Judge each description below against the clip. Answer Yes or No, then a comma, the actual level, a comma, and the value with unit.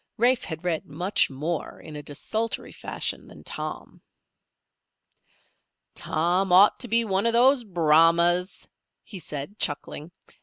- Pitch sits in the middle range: Yes, medium, 180 Hz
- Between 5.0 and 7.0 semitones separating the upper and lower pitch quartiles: Yes, wide, 5.4 semitones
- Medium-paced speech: No, slow, 125 wpm